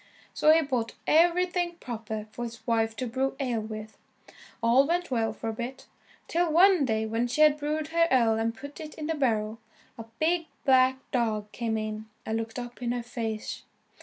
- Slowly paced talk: No, average, 195 wpm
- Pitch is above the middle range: Yes, high, 245 Hz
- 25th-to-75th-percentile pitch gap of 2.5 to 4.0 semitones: No, average, 5.3 semitones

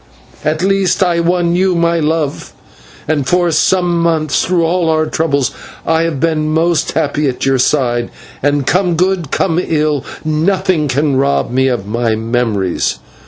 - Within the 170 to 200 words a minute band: No, average, 160 wpm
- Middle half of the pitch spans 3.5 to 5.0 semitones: Yes, average, 3.9 semitones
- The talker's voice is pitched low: No, medium, 155 Hz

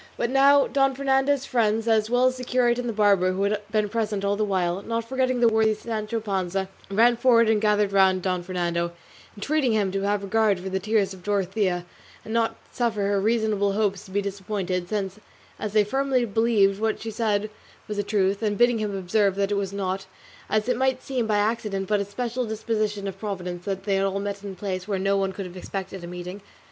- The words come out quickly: Yes, fast, 225 wpm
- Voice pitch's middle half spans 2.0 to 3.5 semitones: Yes, average, 2.7 semitones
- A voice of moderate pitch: No, high, 205 Hz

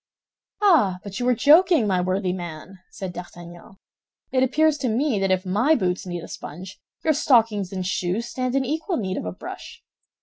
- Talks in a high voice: Yes, high, 200 Hz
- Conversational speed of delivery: Yes, average, 190 wpm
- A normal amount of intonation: No, wide, 6.2 semitones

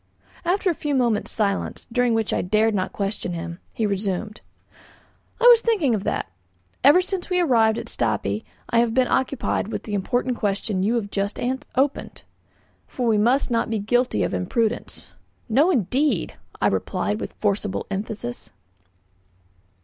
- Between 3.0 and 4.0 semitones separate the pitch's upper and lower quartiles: No, average, 4.4 semitones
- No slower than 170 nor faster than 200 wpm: No, average, 155 wpm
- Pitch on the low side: No, high, 225 Hz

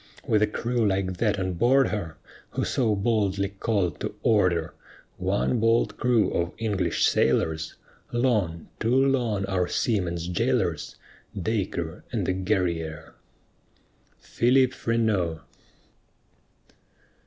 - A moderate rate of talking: No, slow, 110 wpm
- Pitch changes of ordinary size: Yes, average, 4.4 semitones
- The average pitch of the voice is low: Yes, low, 100 Hz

